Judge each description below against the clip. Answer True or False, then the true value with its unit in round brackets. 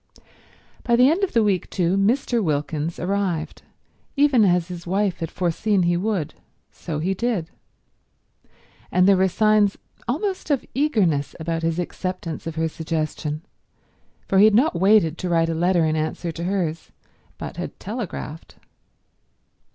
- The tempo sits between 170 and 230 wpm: False (150 wpm)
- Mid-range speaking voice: True (180 Hz)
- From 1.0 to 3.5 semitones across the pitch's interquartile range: False (4.5 semitones)